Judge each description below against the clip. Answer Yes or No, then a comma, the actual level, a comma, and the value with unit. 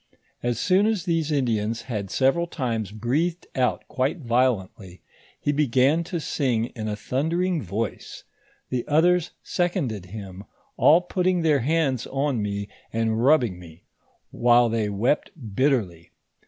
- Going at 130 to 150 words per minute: Yes, average, 140 wpm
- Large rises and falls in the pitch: Yes, wide, 6.4 semitones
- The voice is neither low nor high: No, low, 125 Hz